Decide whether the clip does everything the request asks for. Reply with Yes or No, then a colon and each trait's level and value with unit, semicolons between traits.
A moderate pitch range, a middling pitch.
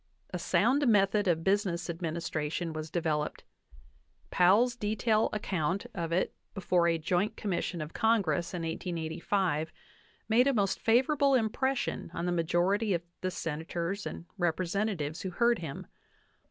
Yes: average, 4.3 semitones; medium, 180 Hz